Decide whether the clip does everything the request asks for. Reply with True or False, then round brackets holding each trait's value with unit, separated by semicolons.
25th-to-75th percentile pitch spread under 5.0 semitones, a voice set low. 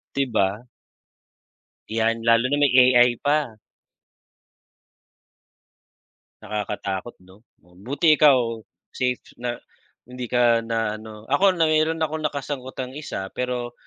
True (4.3 semitones; 125 Hz)